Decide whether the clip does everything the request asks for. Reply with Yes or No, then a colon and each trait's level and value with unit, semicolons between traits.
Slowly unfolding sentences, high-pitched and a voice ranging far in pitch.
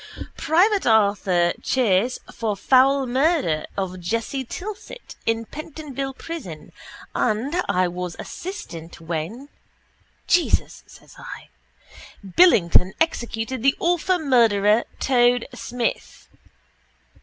Yes: slow, 100 wpm; high, 240 Hz; wide, 6.5 semitones